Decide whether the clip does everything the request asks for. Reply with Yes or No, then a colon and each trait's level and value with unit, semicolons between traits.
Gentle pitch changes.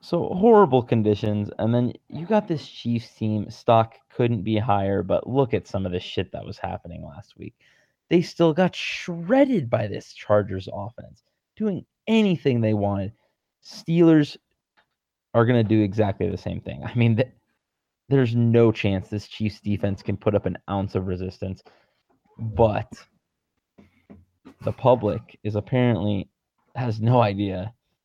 No: average, 4.0 semitones